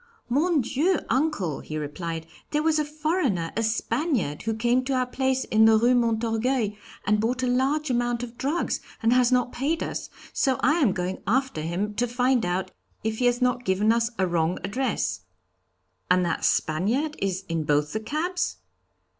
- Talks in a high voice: Yes, high, 240 Hz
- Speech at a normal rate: Yes, average, 180 wpm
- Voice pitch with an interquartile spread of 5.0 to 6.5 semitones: Yes, average, 5.3 semitones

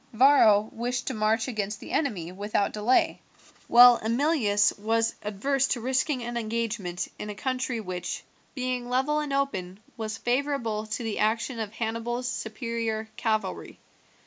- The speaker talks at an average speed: Yes, average, 145 wpm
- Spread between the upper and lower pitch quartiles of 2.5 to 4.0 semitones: Yes, average, 3.0 semitones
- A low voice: No, high, 230 Hz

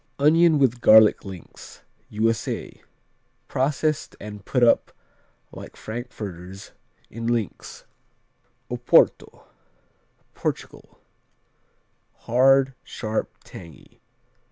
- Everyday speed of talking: No, slow, 75 wpm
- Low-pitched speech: Yes, low, 115 Hz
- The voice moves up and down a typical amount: Yes, average, 4.3 semitones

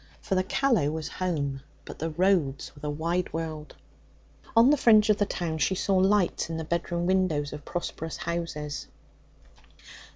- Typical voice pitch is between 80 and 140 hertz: No, medium, 170 Hz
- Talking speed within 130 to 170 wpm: Yes, average, 165 wpm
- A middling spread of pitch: Yes, average, 3.6 semitones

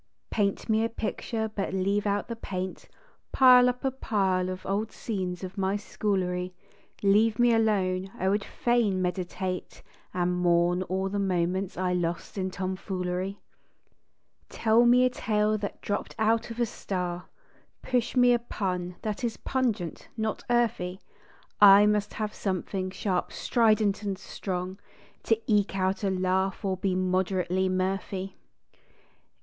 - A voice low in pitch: No, high, 195 Hz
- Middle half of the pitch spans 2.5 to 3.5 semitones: Yes, average, 2.9 semitones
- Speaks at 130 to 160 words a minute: Yes, average, 145 wpm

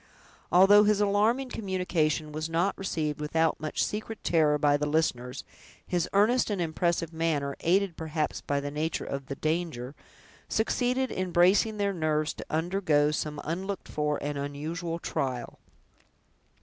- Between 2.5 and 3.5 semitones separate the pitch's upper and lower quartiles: No, average, 4.5 semitones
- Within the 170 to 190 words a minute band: No, average, 145 wpm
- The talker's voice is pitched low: No, medium, 165 Hz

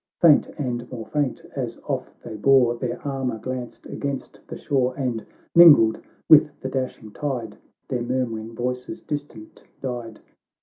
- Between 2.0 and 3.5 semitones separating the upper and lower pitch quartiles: Yes, narrow, 2.6 semitones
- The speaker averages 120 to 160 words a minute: Yes, average, 140 wpm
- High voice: No, low, 125 Hz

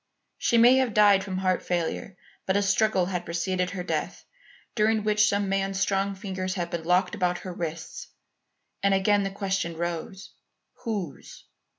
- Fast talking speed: No, average, 165 wpm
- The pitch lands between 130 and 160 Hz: No, high, 195 Hz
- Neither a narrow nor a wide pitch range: No, narrow, 2.2 semitones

